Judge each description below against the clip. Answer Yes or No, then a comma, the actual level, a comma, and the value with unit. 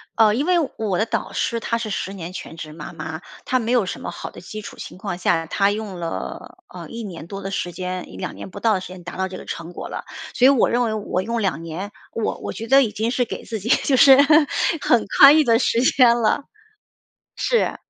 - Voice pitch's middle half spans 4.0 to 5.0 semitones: Yes, average, 4.3 semitones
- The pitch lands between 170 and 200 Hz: No, high, 210 Hz